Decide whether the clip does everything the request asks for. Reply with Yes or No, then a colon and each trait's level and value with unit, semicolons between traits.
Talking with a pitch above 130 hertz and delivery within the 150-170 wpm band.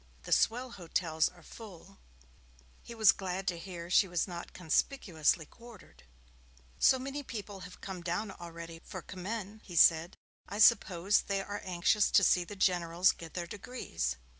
Yes: medium, 185 Hz; average, 160 wpm